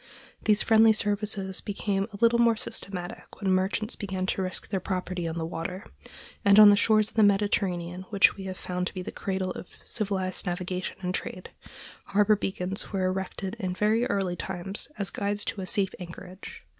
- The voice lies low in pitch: No, high, 195 Hz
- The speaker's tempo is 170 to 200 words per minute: Yes, average, 185 wpm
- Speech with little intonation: Yes, narrow, 2.0 semitones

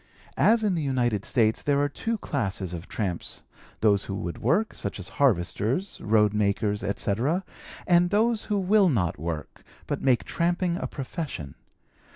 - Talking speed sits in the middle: Yes, average, 160 wpm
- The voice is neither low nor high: No, low, 125 Hz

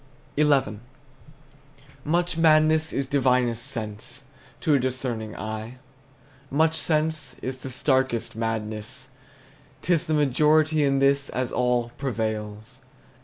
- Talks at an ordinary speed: No, slow, 110 wpm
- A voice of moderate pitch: No, low, 130 Hz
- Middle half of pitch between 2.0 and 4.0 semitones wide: No, average, 4.7 semitones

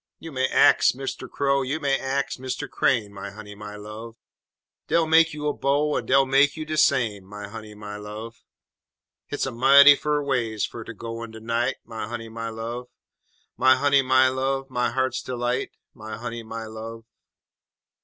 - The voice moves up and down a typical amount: Yes, average, 3.6 semitones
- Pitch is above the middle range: No, low, 120 Hz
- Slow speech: No, average, 185 wpm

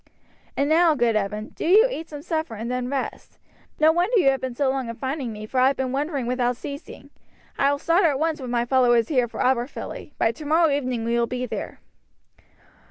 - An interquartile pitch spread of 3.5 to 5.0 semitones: Yes, average, 4.0 semitones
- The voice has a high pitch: Yes, very high, 265 Hz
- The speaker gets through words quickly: Yes, fast, 220 wpm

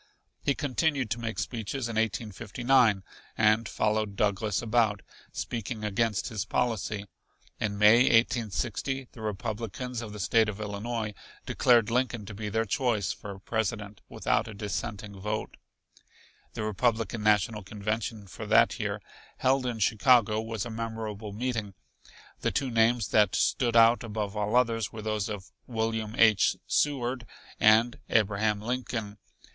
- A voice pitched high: No, low, 110 Hz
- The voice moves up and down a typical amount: No, narrow, 2.1 semitones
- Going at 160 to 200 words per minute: No, average, 140 wpm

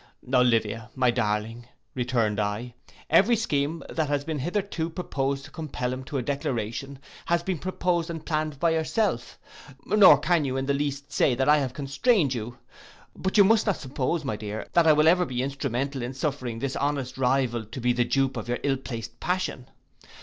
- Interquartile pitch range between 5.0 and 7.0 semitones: No, average, 4.5 semitones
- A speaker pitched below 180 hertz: Yes, low, 135 Hz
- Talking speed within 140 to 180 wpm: No, average, 190 wpm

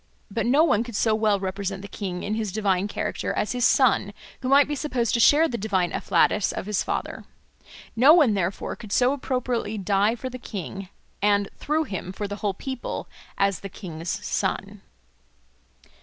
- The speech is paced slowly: No, average, 185 wpm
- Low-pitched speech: No, high, 210 Hz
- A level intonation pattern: No, average, 4.2 semitones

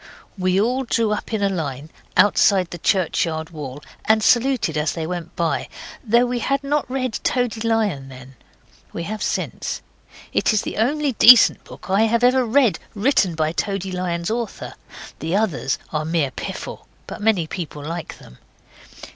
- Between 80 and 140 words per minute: No, average, 165 wpm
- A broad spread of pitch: Yes, wide, 6.2 semitones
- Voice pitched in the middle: No, high, 200 Hz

